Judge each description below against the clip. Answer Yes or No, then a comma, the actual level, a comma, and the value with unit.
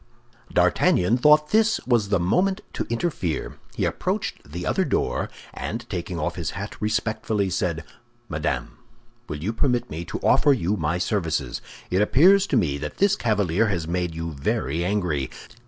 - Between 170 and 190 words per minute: No, average, 160 wpm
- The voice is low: Yes, very low, 95 Hz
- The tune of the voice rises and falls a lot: Yes, wide, 6.3 semitones